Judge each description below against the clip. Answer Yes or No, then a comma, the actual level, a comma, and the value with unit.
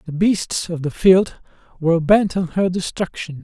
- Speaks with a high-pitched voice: No, medium, 175 Hz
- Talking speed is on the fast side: No, average, 175 wpm